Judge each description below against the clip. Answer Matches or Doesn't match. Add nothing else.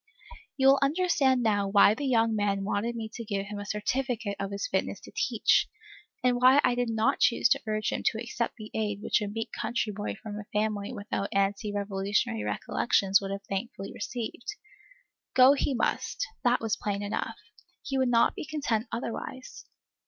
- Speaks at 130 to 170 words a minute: Doesn't match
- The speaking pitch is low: Doesn't match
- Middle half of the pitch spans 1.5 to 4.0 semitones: Matches